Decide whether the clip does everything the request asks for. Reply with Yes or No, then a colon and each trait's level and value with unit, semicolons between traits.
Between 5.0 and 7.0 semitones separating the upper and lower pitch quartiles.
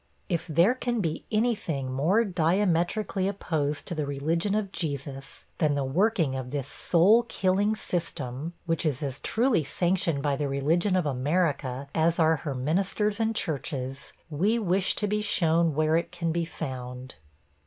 Yes: average, 5.3 semitones